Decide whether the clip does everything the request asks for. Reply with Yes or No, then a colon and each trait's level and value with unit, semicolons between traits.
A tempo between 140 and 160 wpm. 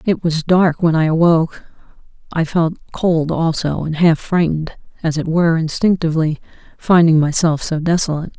Yes: average, 150 wpm